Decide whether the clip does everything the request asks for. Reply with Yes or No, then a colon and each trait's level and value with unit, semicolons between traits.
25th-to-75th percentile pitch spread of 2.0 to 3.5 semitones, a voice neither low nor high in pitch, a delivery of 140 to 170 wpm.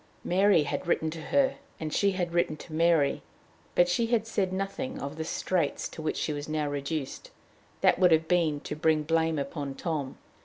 No: average, 3.2 semitones; medium, 160 Hz; average, 190 wpm